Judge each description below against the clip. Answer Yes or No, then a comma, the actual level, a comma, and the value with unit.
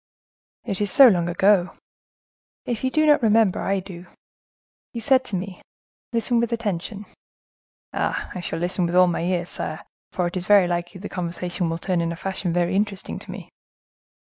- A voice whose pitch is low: No, medium, 185 Hz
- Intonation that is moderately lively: Yes, average, 3.2 semitones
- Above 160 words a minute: Yes, average, 180 wpm